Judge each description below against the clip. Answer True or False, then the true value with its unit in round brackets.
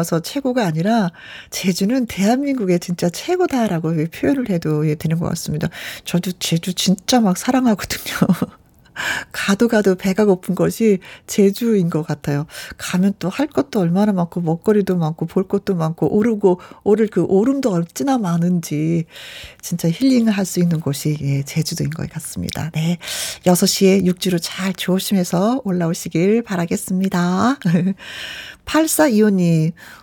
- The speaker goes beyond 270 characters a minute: True (285 characters per minute)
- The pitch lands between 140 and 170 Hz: False (185 Hz)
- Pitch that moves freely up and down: False (4.1 semitones)